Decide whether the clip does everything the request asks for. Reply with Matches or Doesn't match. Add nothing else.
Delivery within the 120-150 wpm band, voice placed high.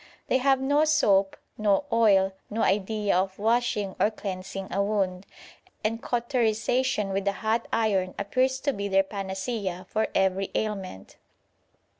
Matches